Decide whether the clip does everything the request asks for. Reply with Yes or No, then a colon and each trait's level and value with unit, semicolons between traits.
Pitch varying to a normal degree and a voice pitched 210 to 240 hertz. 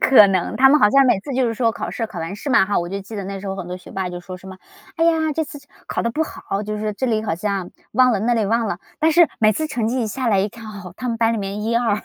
Yes: average, 4.4 semitones; high, 220 Hz